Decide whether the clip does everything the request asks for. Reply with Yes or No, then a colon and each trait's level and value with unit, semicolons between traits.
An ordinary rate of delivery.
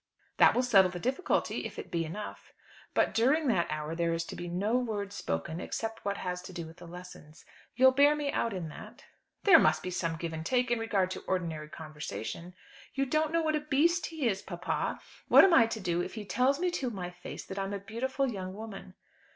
No: fast, 225 wpm